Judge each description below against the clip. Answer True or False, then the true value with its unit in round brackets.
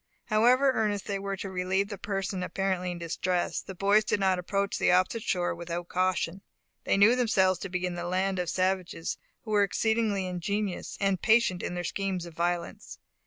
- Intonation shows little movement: True (2.0 semitones)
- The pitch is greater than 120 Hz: True (190 Hz)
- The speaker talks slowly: False (190 wpm)